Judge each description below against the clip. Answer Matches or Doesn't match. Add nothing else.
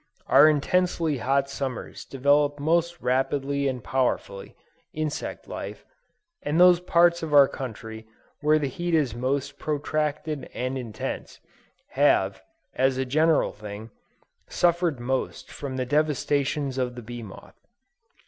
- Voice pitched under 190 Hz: Matches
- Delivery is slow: Matches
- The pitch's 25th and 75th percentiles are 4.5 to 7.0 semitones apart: Doesn't match